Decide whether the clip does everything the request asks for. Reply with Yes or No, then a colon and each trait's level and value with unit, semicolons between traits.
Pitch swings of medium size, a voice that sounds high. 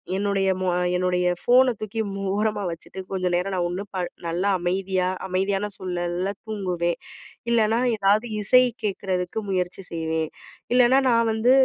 Yes: average, 3.0 semitones; high, 195 Hz